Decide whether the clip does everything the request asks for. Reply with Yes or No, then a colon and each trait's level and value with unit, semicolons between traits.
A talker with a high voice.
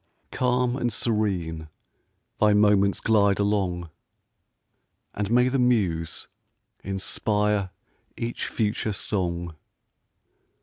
No: low, 105 Hz